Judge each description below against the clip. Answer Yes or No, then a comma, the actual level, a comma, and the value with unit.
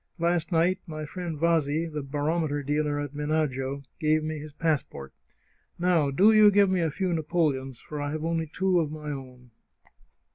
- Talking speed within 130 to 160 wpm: No, average, 175 wpm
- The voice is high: No, medium, 155 Hz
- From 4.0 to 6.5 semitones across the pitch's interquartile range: No, narrow, 2.6 semitones